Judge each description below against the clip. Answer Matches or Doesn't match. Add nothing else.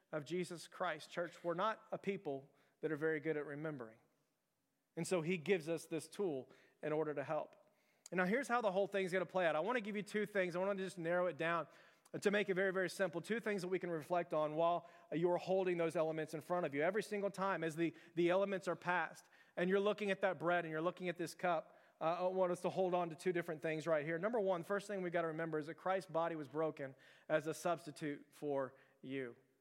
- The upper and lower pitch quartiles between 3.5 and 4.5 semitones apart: Doesn't match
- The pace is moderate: Doesn't match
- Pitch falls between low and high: Matches